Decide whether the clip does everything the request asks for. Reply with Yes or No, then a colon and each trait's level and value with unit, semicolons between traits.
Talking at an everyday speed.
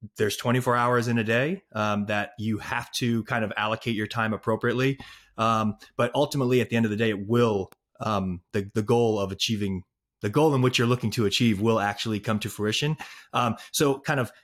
No: fast, 215 wpm